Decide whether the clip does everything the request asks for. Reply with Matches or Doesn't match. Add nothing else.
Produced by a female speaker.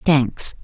Matches